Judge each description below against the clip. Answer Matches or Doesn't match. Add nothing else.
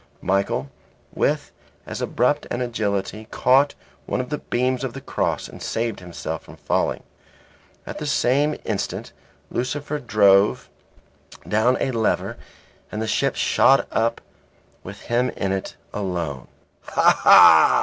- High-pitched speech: Doesn't match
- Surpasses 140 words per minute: Doesn't match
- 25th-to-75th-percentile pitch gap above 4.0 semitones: Matches